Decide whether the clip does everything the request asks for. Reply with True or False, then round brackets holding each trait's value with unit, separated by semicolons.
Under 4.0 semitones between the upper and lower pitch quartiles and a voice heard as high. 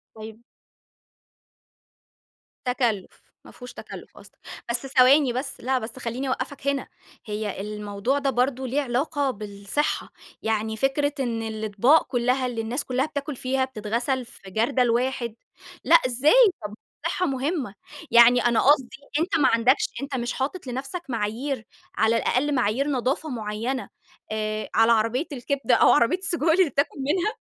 True (3.6 semitones; 255 Hz)